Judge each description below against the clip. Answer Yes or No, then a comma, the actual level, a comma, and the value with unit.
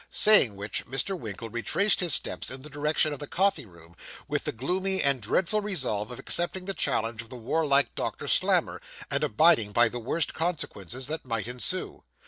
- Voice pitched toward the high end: No, low, 135 Hz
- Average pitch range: No, wide, 7.2 semitones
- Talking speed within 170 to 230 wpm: Yes, average, 185 wpm